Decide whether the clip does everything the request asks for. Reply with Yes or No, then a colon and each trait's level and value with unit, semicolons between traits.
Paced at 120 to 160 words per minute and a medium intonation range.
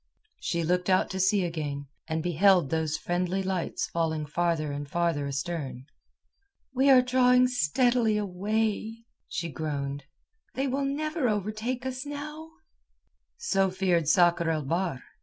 No: slow, 135 wpm; wide, 7.1 semitones